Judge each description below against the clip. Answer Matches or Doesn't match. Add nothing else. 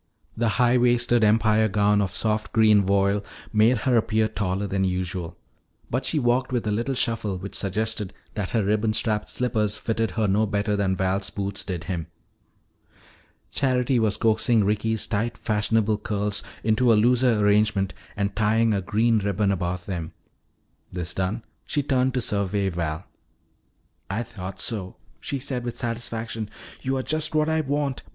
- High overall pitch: Doesn't match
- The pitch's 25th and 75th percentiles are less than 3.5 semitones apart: Matches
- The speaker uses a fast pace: Doesn't match